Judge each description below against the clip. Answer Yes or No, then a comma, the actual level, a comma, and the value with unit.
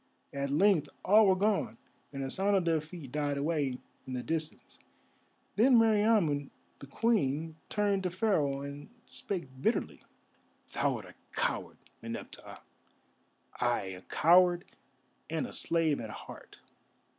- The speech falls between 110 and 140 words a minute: Yes, slow, 135 wpm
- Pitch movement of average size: No, wide, 5.7 semitones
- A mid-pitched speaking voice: Yes, medium, 160 Hz